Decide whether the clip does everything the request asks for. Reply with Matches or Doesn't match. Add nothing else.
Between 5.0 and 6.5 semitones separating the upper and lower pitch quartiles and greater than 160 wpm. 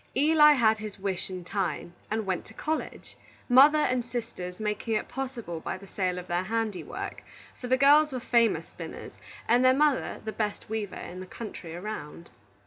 Matches